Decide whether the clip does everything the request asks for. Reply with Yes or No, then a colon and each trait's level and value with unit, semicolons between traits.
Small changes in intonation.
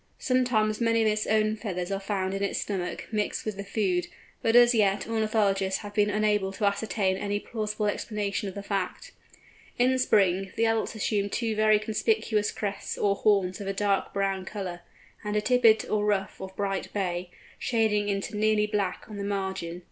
Yes: narrow, 1.8 semitones